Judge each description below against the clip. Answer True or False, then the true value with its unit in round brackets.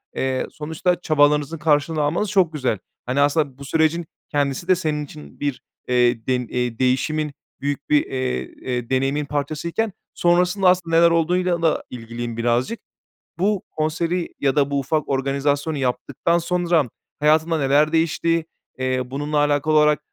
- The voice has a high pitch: False (150 Hz)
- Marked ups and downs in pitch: False (3.6 semitones)